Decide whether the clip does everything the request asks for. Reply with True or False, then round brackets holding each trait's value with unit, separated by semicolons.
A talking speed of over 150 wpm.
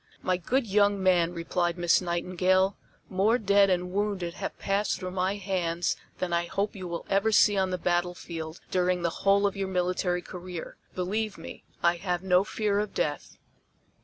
True (175 wpm)